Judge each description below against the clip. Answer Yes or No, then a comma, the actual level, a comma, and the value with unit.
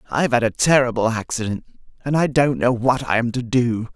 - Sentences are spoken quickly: Yes, fast, 210 wpm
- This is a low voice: Yes, low, 120 Hz